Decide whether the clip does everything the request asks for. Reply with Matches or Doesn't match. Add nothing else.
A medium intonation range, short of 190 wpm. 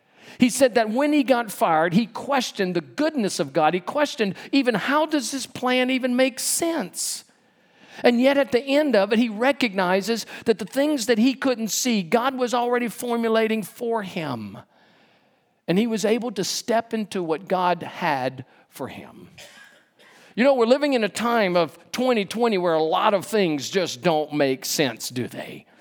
Matches